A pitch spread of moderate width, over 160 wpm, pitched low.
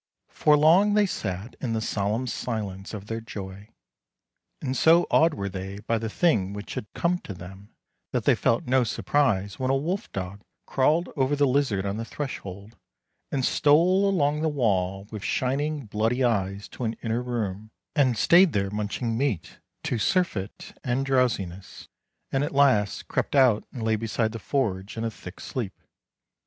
No: wide, 5.8 semitones; average, 170 wpm; low, 115 Hz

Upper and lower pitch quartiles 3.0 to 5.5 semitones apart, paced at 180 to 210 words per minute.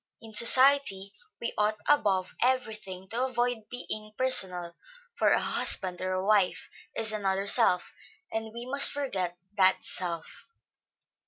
No: average, 4.6 semitones; average, 140 wpm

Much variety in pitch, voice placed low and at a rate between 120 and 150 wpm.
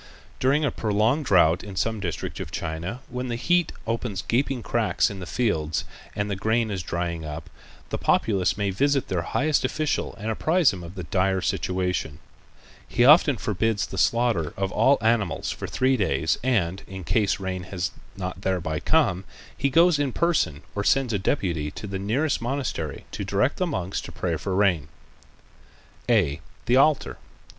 No: wide, 5.8 semitones; low, 100 Hz; average, 175 wpm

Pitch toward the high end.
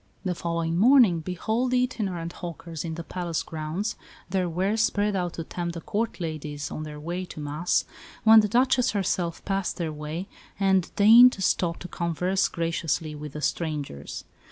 No: medium, 175 Hz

